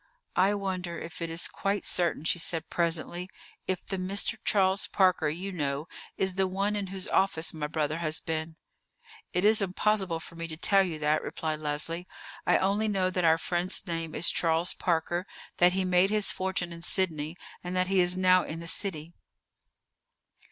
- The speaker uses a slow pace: No, average, 185 wpm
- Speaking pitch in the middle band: Yes, medium, 180 Hz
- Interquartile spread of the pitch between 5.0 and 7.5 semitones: No, average, 2.7 semitones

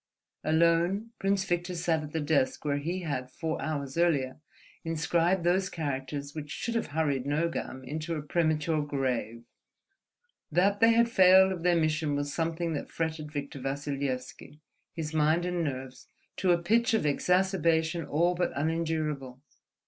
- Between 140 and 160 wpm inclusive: Yes, average, 150 wpm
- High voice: No, medium, 160 Hz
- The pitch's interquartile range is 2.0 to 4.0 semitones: Yes, average, 3.3 semitones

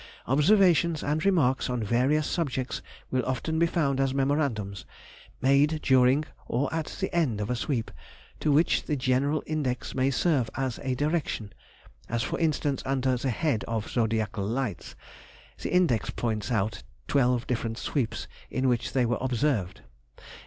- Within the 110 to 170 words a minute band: Yes, average, 145 wpm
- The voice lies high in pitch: No, low, 130 Hz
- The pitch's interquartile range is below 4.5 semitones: Yes, average, 4.1 semitones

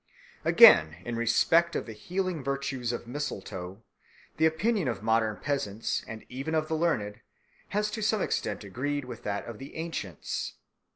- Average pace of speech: Yes, average, 160 wpm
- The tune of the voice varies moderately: No, wide, 6.6 semitones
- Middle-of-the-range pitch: No, low, 130 Hz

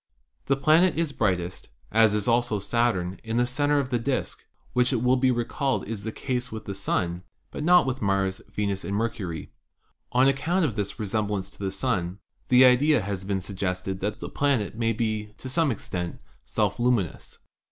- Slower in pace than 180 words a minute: No, average, 195 wpm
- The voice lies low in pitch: Yes, low, 115 Hz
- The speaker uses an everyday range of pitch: Yes, average, 4.7 semitones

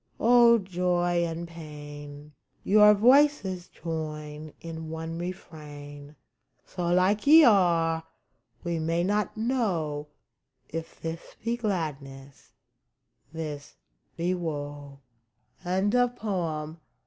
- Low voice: No, medium, 165 Hz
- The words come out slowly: Yes, slow, 90 wpm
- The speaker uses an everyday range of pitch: Yes, average, 4.1 semitones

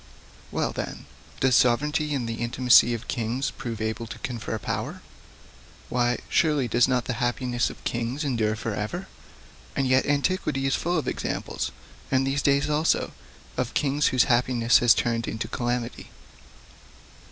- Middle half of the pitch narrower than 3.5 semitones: Yes, narrow, 2.6 semitones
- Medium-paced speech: Yes, average, 150 wpm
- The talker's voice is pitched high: No, low, 125 Hz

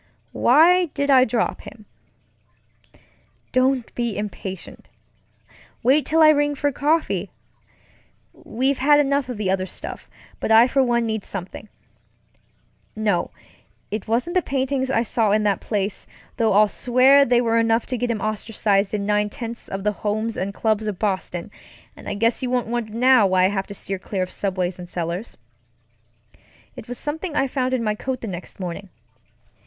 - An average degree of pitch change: Yes, average, 4.2 semitones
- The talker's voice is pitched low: No, high, 225 Hz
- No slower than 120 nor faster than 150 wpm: No, average, 170 wpm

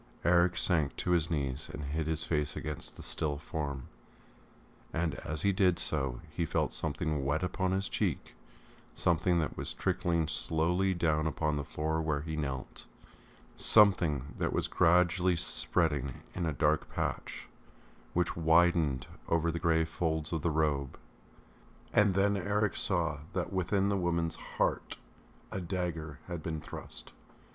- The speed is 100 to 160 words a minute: Yes, average, 150 wpm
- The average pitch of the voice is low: Yes, very low, 80 Hz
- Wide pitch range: No, narrow, 2.5 semitones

